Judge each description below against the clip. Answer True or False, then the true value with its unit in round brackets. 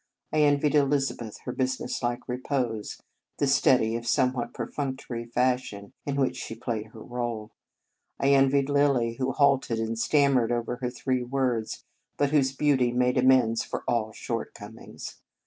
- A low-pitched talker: True (125 Hz)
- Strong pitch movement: False (2.7 semitones)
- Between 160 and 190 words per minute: False (145 wpm)